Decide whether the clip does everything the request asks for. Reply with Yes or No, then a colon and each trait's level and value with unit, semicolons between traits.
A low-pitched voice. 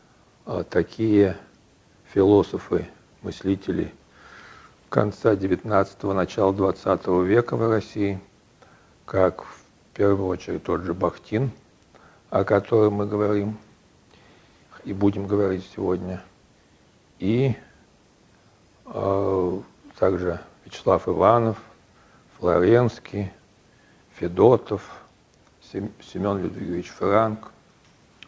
Yes: low, 100 Hz